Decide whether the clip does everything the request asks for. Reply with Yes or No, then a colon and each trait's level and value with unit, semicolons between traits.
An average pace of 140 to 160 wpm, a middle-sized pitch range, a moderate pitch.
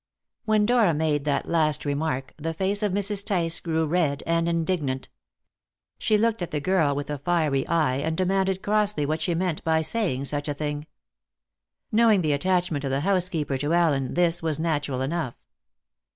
No: average, 175 wpm; average, 4.1 semitones; medium, 160 Hz